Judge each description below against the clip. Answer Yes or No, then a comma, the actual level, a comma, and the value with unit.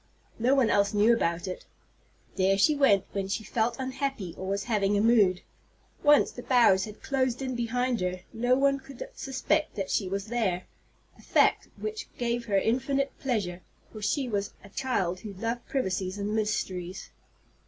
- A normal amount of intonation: Yes, average, 4.7 semitones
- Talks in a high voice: Yes, high, 220 Hz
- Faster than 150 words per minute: Yes, average, 175 wpm